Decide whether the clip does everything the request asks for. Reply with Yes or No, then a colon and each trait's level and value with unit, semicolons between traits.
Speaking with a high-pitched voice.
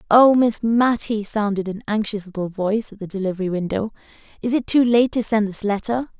Yes: high, 215 Hz